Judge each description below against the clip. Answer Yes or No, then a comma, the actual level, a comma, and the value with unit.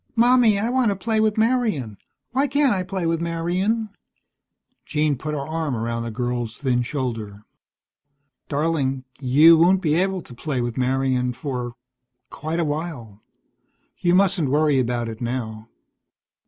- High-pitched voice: No, medium, 150 Hz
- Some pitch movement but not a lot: No, wide, 7.2 semitones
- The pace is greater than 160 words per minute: No, average, 150 wpm